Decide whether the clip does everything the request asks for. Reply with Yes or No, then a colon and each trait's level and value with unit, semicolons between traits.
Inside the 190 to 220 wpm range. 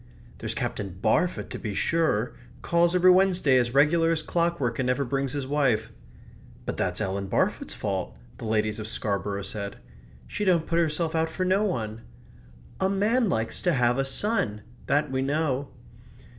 No: average, 170 wpm